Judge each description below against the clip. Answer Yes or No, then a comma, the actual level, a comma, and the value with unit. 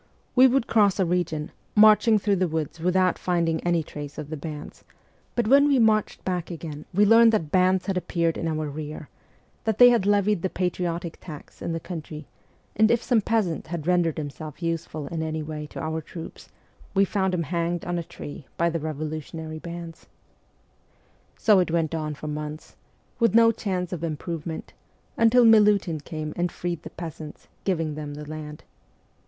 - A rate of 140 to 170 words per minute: No, average, 180 wpm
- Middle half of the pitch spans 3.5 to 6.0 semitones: Yes, average, 3.8 semitones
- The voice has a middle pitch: Yes, medium, 170 Hz